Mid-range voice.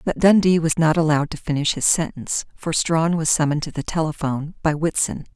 Yes: medium, 155 Hz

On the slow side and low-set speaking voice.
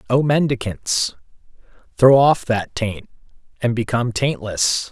Yes: slow, 110 wpm; low, 120 Hz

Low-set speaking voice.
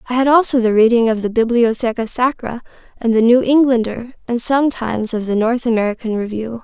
No: high, 235 Hz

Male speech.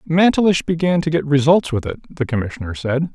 Yes: male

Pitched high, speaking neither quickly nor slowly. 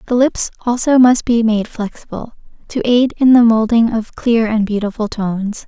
Yes: high, 230 Hz; average, 180 wpm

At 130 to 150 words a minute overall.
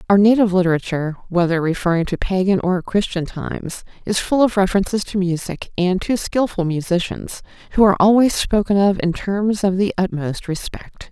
No: average, 165 wpm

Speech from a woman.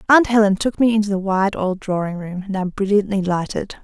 Yes: female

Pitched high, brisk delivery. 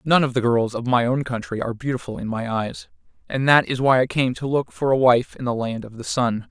No: low, 125 Hz; fast, 275 wpm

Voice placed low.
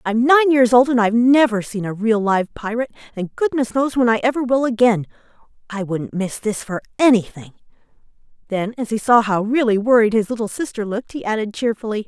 No: high, 225 Hz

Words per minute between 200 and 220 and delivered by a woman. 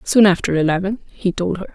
Yes: fast, 205 wpm; female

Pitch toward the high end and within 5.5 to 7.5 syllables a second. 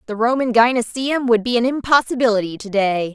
Yes: high, 235 Hz; 5.7 syllables/s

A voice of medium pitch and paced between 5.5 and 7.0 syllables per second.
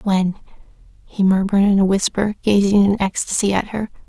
No: high, 200 Hz; 5.6 syllables/s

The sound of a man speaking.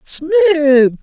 Yes: male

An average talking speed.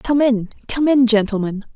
Yes: average, 170 wpm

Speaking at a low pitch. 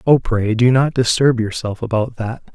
Yes: low, 120 Hz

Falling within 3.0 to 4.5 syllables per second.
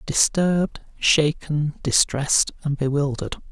Yes: 4.3 syllables/s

